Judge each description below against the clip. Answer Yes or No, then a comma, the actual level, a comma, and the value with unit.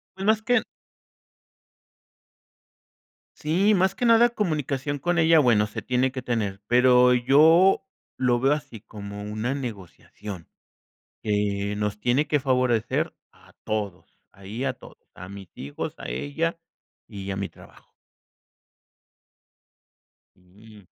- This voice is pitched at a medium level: No, low, 125 Hz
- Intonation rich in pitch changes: Yes, wide, 6.6 semitones